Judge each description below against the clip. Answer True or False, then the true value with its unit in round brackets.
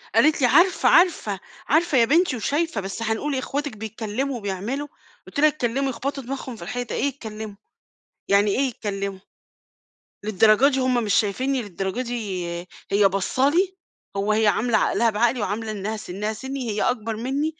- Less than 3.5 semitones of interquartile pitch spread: False (4.6 semitones)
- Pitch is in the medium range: False (230 Hz)